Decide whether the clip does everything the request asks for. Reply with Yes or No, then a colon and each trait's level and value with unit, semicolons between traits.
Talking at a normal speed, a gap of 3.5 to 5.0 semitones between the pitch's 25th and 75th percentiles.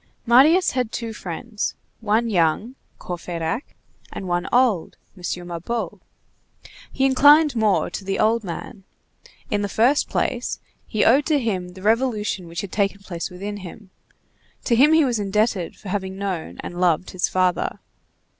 Yes: average, 155 wpm; average, 4.5 semitones